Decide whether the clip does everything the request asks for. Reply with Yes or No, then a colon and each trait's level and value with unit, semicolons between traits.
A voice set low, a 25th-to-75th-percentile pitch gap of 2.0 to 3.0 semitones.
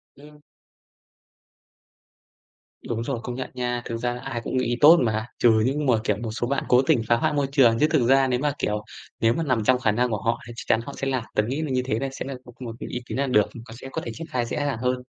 Yes: low, 125 Hz; narrow, 2.6 semitones